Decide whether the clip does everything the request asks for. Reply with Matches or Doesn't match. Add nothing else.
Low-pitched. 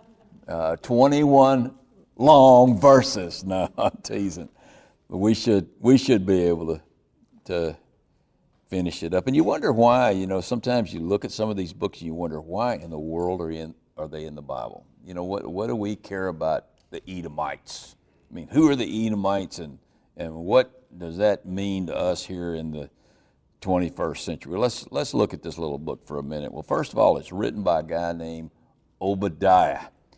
Matches